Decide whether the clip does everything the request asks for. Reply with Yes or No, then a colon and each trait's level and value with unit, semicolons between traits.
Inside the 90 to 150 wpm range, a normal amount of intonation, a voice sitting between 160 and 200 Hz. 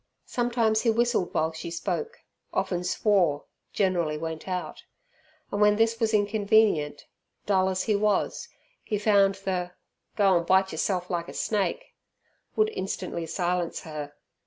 Yes: average, 140 wpm; average, 3.6 semitones; high, 190 Hz